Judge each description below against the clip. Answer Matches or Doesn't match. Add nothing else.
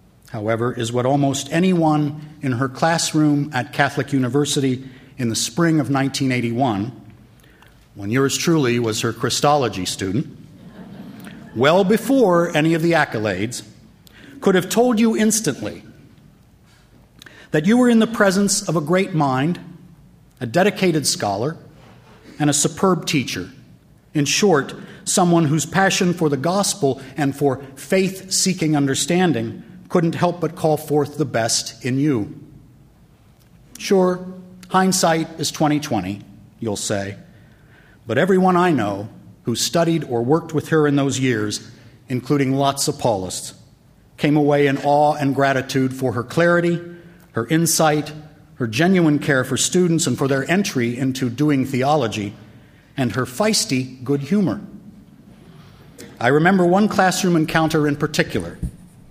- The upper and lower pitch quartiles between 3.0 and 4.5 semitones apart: Doesn't match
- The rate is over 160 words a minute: Doesn't match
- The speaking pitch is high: Doesn't match